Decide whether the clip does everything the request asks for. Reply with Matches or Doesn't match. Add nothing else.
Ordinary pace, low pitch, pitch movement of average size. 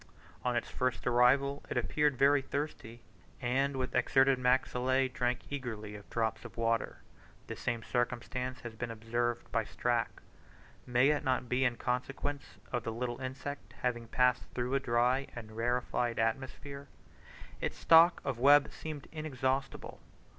Doesn't match